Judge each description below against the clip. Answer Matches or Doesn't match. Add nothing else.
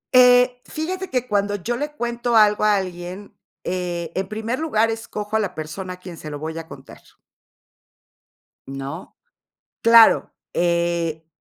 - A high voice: Matches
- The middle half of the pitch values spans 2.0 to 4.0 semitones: Doesn't match